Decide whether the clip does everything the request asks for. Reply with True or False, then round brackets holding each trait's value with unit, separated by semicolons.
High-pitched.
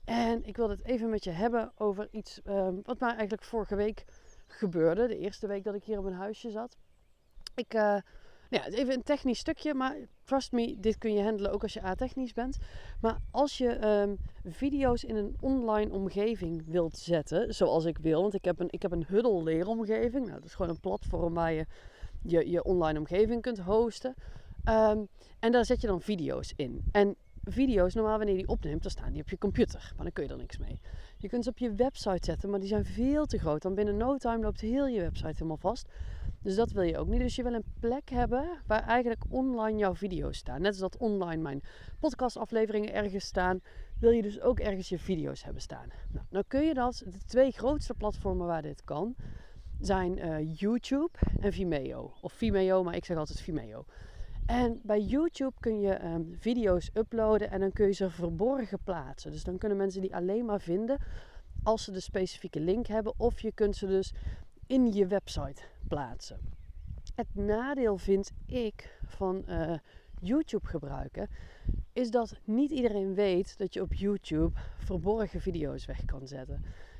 True (210 Hz)